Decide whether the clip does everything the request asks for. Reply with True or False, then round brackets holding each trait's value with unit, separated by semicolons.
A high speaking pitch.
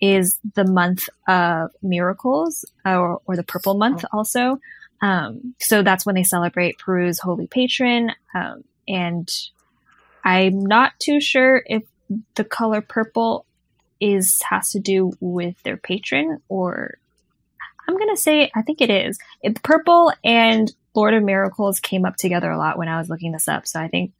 True (200 Hz)